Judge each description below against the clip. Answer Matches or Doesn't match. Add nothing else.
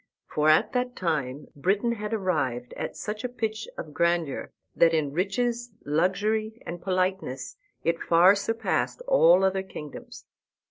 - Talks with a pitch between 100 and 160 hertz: Doesn't match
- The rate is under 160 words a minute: Matches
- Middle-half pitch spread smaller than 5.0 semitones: Doesn't match